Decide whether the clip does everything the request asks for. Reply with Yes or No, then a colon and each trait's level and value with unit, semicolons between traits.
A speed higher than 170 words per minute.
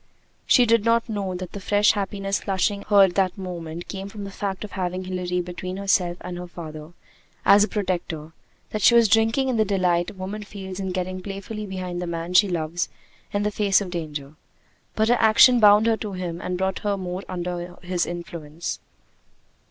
Yes: average, 200 wpm